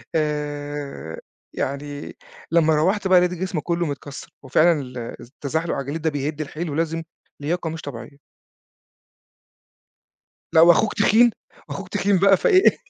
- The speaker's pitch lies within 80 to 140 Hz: No, medium, 160 Hz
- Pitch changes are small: No, average, 3.4 semitones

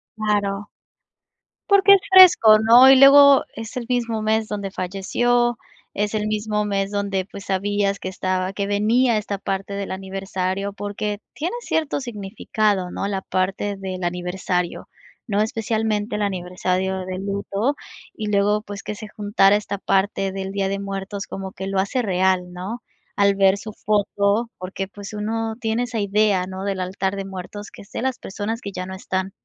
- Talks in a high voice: Yes, high, 200 Hz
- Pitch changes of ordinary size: No, narrow, 2.1 semitones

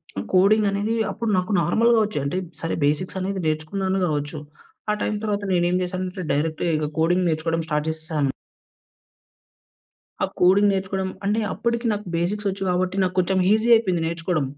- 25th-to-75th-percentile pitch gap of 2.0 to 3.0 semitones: No, average, 3.7 semitones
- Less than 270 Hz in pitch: Yes, medium, 185 Hz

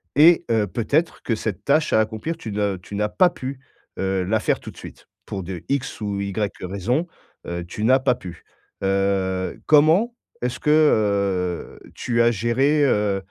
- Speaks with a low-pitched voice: Yes, low, 110 Hz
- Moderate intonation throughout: No, wide, 6.2 semitones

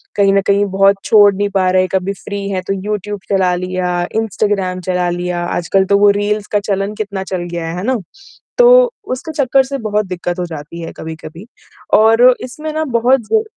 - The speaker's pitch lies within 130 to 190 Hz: No, high, 200 Hz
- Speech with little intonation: No, average, 3.1 semitones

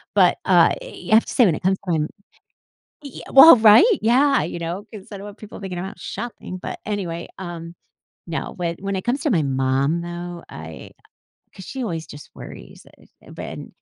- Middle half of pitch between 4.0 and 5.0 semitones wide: Yes, average, 4.6 semitones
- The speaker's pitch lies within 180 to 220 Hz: Yes, medium, 185 Hz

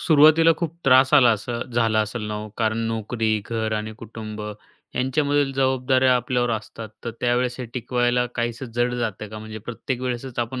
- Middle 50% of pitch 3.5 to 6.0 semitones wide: No, average, 2.7 semitones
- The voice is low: Yes, low, 120 Hz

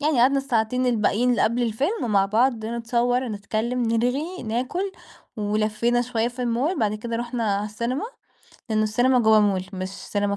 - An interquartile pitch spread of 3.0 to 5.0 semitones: No, narrow, 2.6 semitones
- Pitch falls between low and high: No, high, 235 Hz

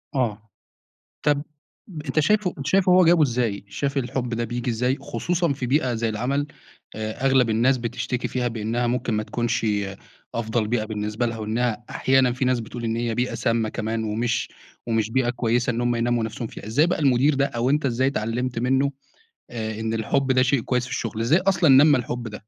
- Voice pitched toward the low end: Yes, low, 120 Hz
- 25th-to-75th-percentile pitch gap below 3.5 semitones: Yes, average, 2.8 semitones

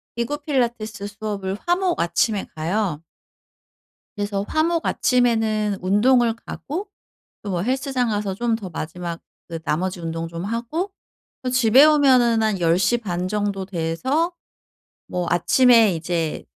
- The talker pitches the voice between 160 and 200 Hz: No, high, 215 Hz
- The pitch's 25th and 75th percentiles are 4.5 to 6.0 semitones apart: Yes, wide, 5.6 semitones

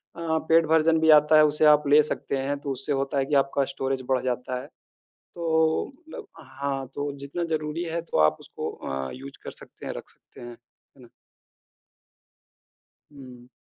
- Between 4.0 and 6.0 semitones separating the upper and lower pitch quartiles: No, average, 3.0 semitones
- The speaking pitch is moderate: Yes, medium, 145 Hz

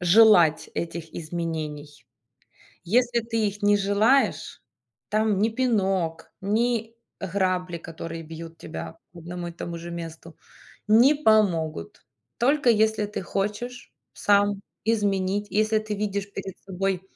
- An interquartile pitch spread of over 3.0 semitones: Yes, average, 4.3 semitones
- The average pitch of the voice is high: Yes, high, 195 Hz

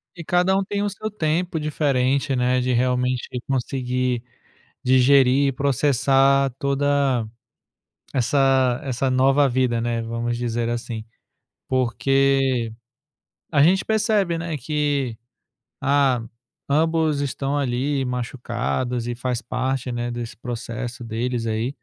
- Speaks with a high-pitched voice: No, low, 130 Hz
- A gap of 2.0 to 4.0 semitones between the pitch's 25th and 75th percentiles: Yes, average, 2.8 semitones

